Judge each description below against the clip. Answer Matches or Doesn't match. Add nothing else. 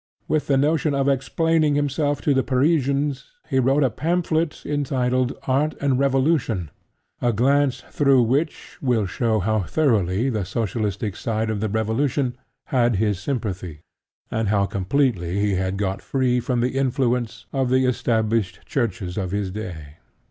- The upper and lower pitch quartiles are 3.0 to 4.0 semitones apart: Doesn't match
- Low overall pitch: Matches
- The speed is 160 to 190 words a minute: Doesn't match